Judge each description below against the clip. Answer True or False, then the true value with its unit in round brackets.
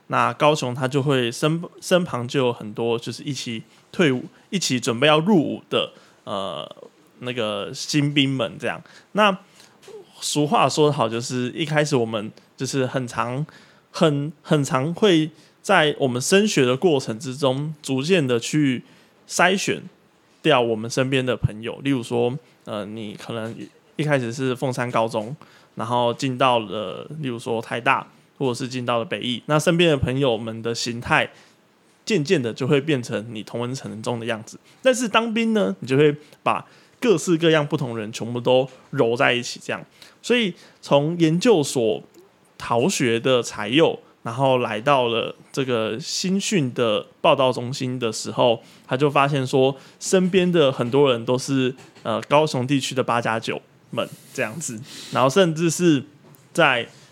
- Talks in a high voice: False (135 Hz)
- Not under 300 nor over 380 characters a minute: False (235 characters per minute)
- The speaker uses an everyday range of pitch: True (4.5 semitones)